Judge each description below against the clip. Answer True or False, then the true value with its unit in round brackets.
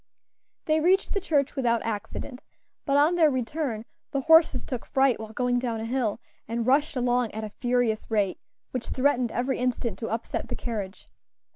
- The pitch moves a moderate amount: True (3.5 semitones)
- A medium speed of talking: True (175 wpm)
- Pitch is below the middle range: False (250 Hz)